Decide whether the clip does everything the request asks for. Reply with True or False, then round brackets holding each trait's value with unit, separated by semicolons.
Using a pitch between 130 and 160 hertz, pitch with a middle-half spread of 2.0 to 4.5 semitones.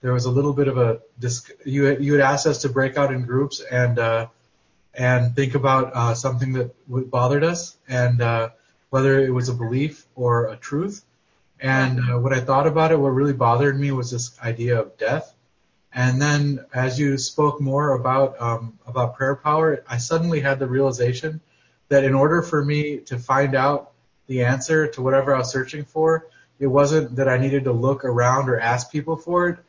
True (135 Hz; 2.5 semitones)